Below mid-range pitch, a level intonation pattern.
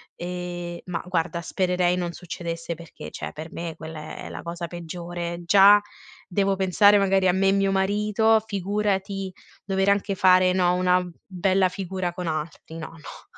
No: medium, 180 Hz; narrow, 2.1 semitones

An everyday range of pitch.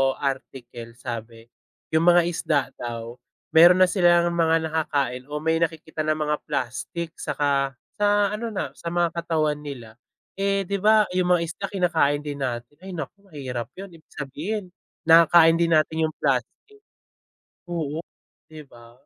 Yes: average, 4.0 semitones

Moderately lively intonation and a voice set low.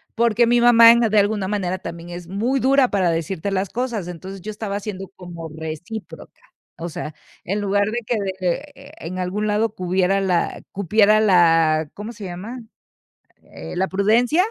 No: average, 3.8 semitones; high, 200 Hz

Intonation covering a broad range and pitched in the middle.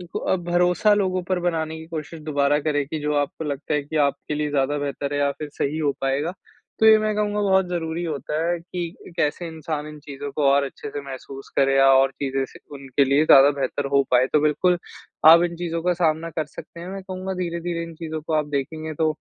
No: average, 3.3 semitones; medium, 155 Hz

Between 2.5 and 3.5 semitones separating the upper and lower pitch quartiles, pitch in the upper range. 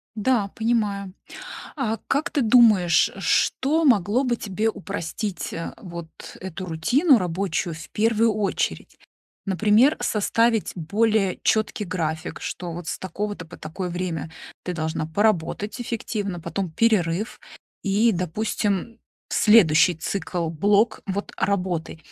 No: average, 4.3 semitones; high, 200 Hz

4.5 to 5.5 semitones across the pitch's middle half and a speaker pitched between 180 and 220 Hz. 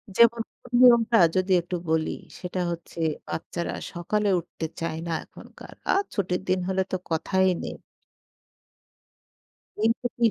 Yes: average, 4.8 semitones; medium, 185 Hz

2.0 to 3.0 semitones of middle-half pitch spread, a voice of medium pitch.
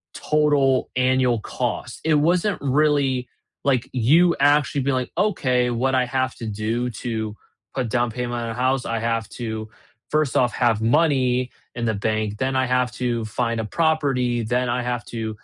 No: narrow, 2.6 semitones; low, 125 Hz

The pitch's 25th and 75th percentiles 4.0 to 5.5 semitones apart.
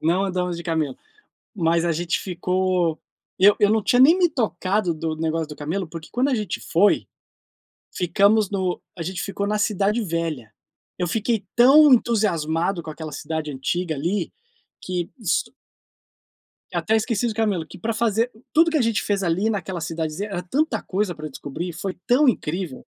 Yes: average, 4.6 semitones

